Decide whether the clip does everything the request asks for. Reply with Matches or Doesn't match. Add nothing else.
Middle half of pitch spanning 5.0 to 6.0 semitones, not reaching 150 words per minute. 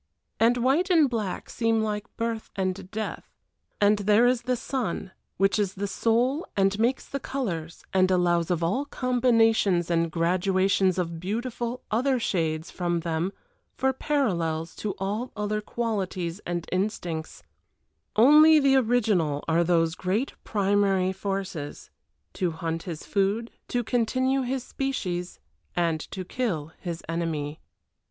Matches